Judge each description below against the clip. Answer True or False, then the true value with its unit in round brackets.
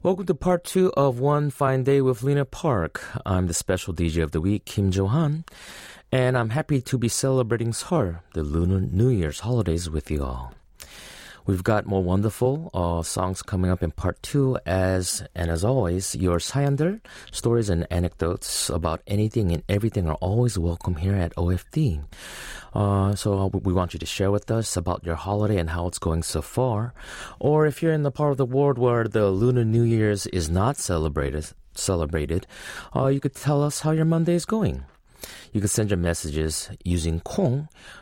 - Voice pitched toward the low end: True (100 Hz)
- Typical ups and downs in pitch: False (6.9 semitones)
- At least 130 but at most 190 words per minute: True (185 wpm)